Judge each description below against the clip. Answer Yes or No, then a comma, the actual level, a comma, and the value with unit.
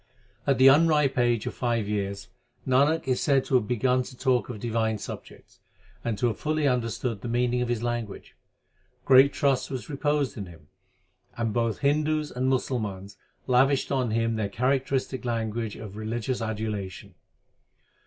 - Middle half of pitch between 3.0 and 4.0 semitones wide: Yes, average, 3.3 semitones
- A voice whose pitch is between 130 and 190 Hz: No, low, 120 Hz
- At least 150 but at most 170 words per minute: Yes, average, 160 wpm